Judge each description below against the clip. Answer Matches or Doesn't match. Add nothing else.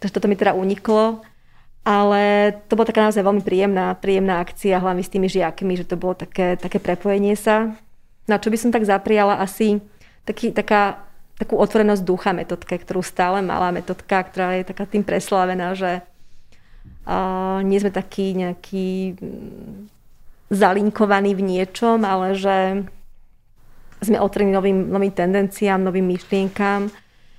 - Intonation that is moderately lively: Doesn't match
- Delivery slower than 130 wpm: Doesn't match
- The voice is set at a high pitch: Matches